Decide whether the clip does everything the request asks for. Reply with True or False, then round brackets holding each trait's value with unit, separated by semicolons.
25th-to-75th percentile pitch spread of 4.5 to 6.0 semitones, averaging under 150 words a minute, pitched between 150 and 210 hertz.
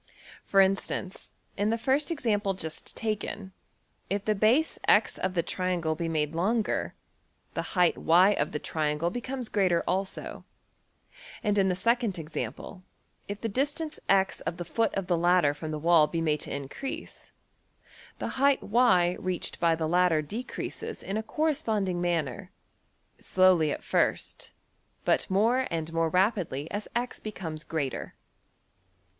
True (4.8 semitones; 140 wpm; 185 Hz)